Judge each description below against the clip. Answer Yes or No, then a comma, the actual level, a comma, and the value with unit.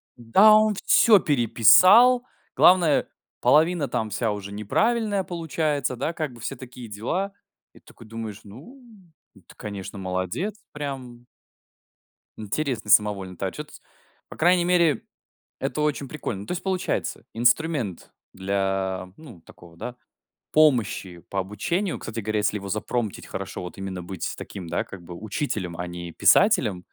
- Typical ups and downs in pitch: No, wide, 8.6 semitones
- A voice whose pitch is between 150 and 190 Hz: No, low, 120 Hz